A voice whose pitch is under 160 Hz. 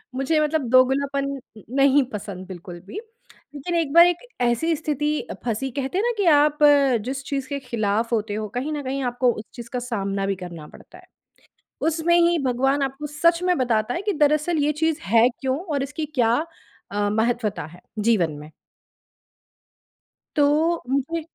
No: very high, 270 Hz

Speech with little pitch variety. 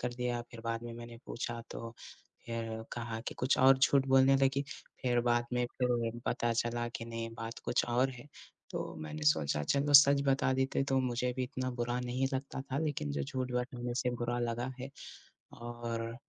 Yes: narrow, 2.1 semitones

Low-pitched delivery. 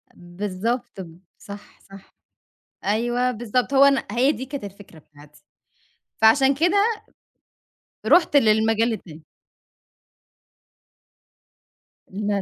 No: high, 220 Hz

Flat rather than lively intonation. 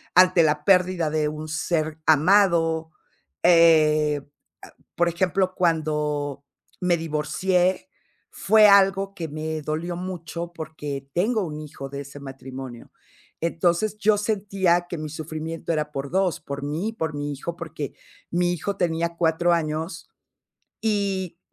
No: average, 3.1 semitones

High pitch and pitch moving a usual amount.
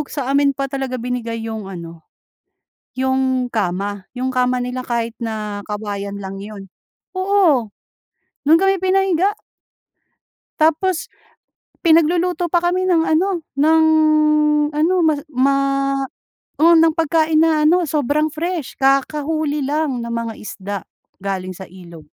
No: very high, 275 Hz; wide, 6.5 semitones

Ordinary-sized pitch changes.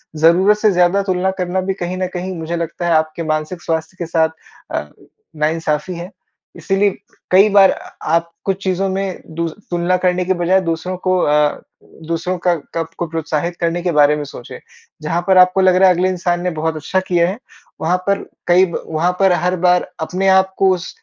No: narrow, 2.3 semitones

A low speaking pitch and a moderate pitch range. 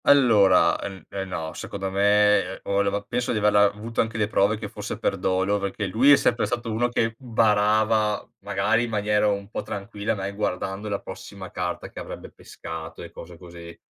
No: low, 100 Hz; narrow, 2.1 semitones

